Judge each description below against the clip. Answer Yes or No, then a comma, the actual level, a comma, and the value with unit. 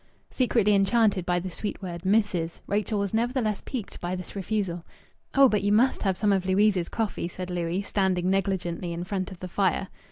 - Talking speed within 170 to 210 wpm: Yes, average, 190 wpm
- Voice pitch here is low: No, high, 195 Hz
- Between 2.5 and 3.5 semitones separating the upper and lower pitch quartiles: Yes, average, 2.8 semitones